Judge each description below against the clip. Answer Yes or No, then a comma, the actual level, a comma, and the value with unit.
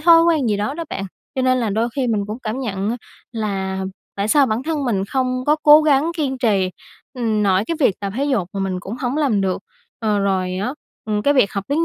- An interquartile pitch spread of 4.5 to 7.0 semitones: Yes, wide, 5.4 semitones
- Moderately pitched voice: No, high, 225 Hz